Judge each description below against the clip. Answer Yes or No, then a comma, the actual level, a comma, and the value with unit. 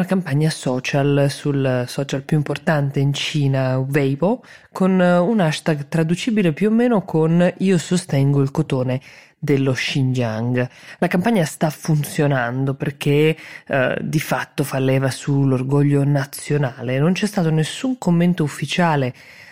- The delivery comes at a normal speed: Yes, average, 130 wpm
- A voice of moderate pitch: Yes, medium, 150 Hz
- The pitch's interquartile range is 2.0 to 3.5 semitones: No, average, 3.9 semitones